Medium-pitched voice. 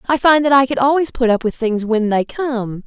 No: high, 245 Hz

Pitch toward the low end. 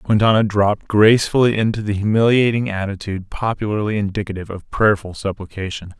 Yes: low, 105 Hz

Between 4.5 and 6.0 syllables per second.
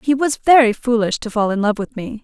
Yes: 5.6 syllables/s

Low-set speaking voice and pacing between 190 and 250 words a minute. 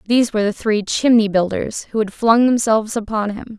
No: high, 220 Hz; average, 200 wpm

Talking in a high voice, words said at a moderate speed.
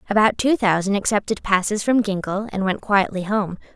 Yes: high, 205 Hz; average, 175 wpm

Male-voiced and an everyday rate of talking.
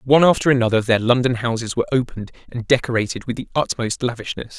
Yes: male; average, 185 wpm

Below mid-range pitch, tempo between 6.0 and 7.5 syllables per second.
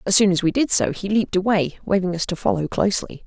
No: high, 190 Hz; 6.5 syllables/s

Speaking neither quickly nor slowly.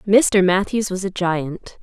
Yes: average, 165 wpm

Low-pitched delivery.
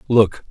Yes: low, 110 Hz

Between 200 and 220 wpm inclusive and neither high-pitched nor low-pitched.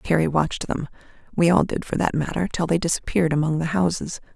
Yes: fast, 205 wpm; medium, 165 Hz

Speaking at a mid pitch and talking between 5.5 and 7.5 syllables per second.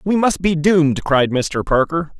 No: medium, 160 Hz; 4.4 syllables/s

